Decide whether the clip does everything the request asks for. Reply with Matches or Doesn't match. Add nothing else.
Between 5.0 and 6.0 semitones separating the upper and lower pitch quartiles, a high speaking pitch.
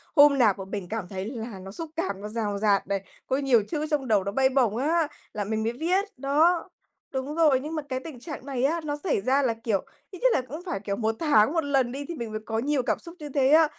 Matches